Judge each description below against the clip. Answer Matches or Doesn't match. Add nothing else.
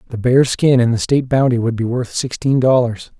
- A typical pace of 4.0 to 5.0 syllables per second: Doesn't match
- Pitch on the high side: Doesn't match